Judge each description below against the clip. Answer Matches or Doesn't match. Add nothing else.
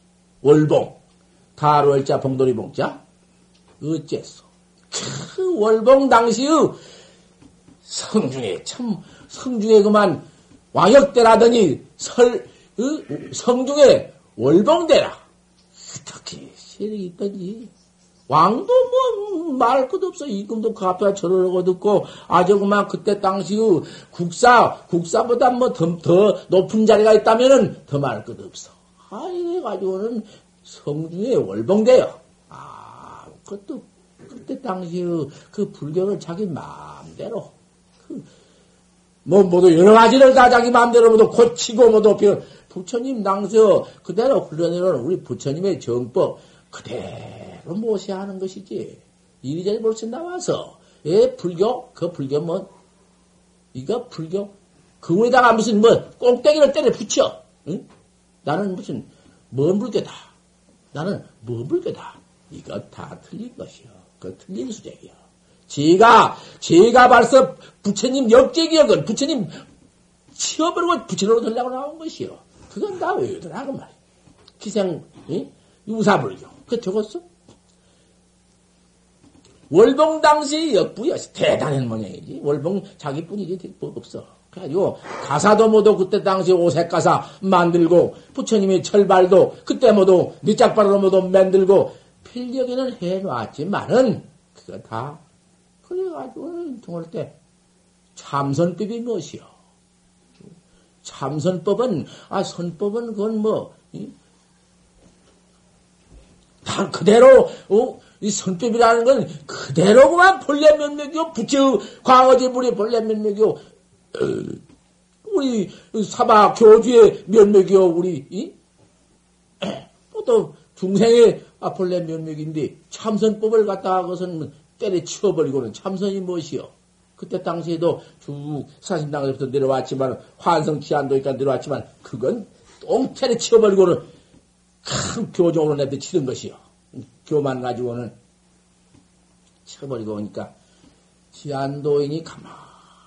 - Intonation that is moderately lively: Doesn't match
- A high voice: Matches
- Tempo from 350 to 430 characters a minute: Doesn't match